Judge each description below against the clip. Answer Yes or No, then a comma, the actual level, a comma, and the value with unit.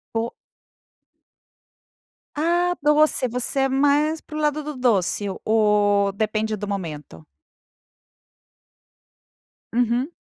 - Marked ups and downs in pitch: Yes, wide, 6.4 semitones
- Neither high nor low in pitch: No, high, 240 Hz